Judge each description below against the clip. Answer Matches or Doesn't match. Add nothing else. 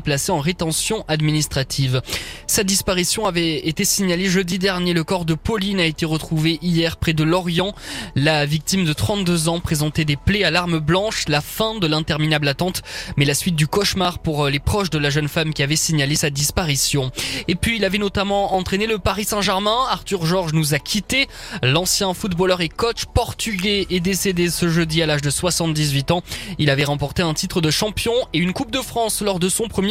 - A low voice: Doesn't match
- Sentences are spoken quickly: Doesn't match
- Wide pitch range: Doesn't match